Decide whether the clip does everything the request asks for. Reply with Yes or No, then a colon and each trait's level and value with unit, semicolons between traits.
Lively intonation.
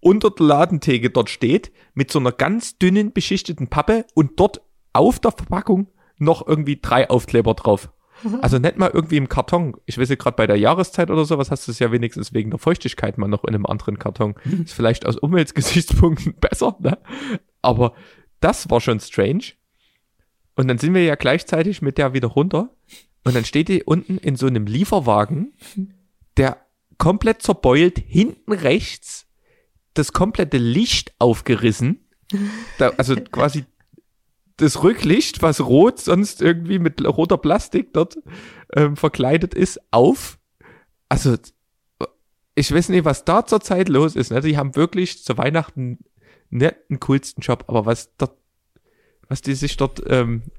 Yes: wide, 6.3 semitones